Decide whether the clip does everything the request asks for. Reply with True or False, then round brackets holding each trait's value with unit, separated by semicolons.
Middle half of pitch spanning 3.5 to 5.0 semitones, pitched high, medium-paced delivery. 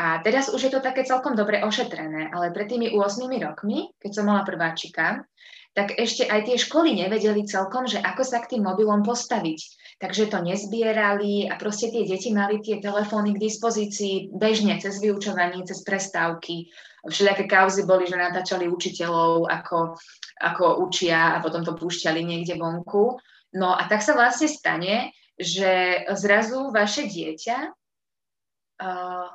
True (4.0 semitones; 200 Hz; 155 wpm)